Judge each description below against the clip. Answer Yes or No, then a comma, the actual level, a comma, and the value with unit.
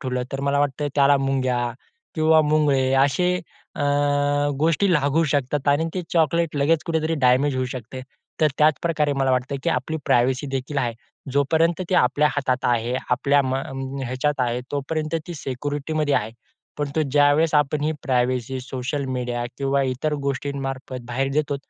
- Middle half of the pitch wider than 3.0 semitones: No, average, 2.7 semitones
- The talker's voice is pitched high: No, medium, 140 Hz